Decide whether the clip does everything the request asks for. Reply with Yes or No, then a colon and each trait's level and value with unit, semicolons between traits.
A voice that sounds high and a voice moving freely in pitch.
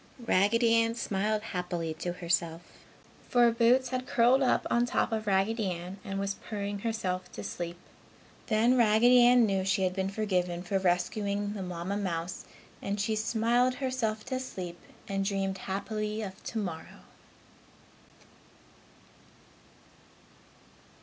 No: high, 205 Hz; average, 3.7 semitones